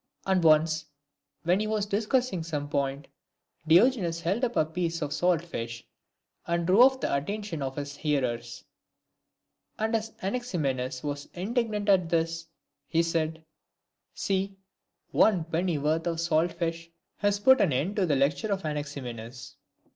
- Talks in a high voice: No, medium, 165 Hz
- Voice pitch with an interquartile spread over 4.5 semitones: Yes, average, 5.1 semitones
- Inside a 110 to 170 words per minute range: Yes, average, 145 wpm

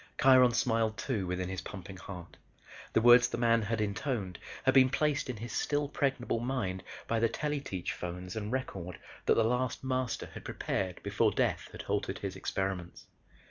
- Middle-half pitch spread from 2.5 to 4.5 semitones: No, average, 5.2 semitones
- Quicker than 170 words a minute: Yes, average, 180 wpm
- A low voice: Yes, low, 115 Hz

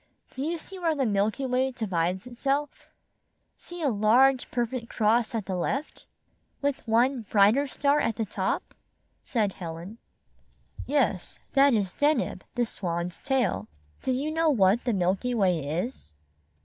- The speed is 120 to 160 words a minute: Yes, average, 150 wpm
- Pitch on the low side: No, high, 235 Hz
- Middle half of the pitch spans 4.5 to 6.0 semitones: Yes, wide, 5.6 semitones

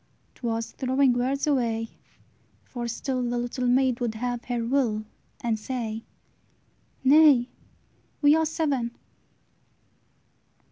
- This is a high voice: Yes, high, 245 Hz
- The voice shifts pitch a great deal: No, narrow, 2.4 semitones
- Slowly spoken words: Yes, slow, 110 wpm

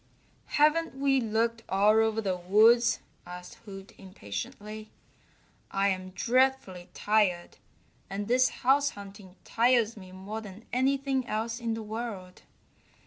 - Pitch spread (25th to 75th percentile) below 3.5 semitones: No, average, 3.9 semitones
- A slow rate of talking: Yes, slow, 120 wpm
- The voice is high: Yes, high, 215 Hz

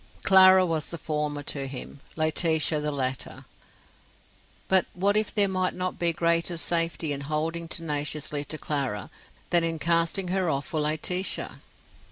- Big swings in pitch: No, average, 3.1 semitones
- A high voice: No, medium, 165 Hz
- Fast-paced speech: No, average, 150 wpm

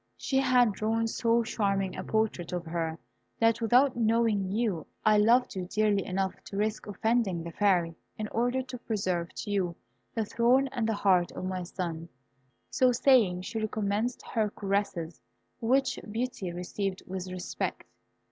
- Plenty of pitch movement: No, average, 3.9 semitones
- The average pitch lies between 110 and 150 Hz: No, high, 210 Hz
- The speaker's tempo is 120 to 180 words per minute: Yes, average, 155 wpm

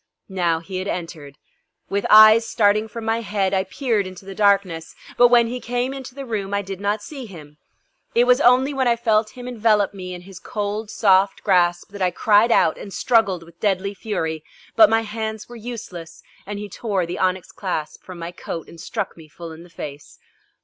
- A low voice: No, high, 200 Hz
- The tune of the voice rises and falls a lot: No, average, 4.0 semitones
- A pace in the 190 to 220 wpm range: Yes, fast, 205 wpm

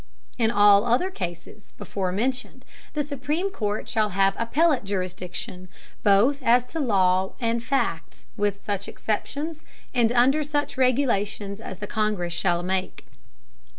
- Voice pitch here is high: Yes, high, 215 Hz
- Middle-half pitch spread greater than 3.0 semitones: Yes, average, 5.2 semitones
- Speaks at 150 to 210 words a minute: No, average, 140 wpm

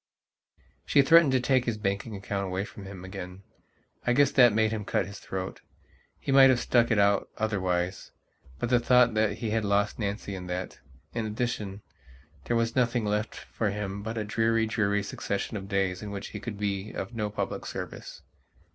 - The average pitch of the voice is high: No, low, 105 Hz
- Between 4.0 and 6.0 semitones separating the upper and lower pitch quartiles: No, average, 2.8 semitones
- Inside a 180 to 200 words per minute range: Yes, average, 190 wpm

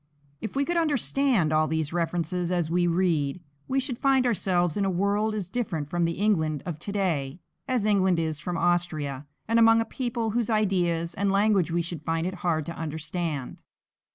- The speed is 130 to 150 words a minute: No, average, 190 wpm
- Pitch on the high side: No, medium, 180 Hz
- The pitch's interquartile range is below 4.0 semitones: No, average, 4.7 semitones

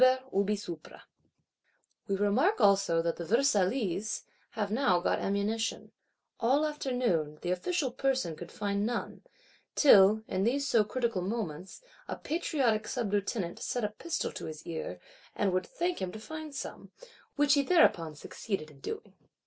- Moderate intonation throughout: No, wide, 6.2 semitones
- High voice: Yes, high, 210 Hz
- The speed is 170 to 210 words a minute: No, average, 140 wpm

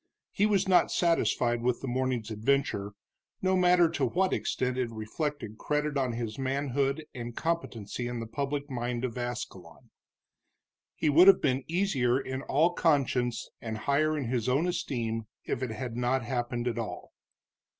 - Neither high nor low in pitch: No, low, 130 Hz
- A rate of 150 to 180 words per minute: Yes, average, 160 wpm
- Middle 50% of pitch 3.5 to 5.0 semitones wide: Yes, average, 3.8 semitones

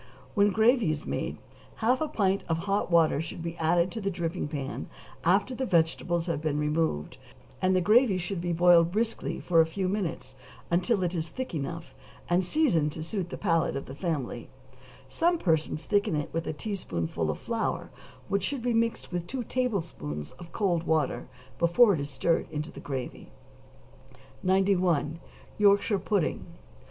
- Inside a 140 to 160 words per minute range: No, average, 170 wpm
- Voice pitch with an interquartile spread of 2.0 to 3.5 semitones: No, average, 4.1 semitones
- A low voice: No, medium, 175 Hz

